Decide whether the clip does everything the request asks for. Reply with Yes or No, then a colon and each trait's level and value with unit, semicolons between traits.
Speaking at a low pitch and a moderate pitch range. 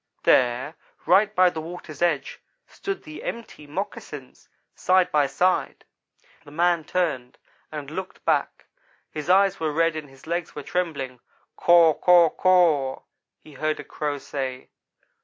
No: medium, 160 Hz; average, 3.8 semitones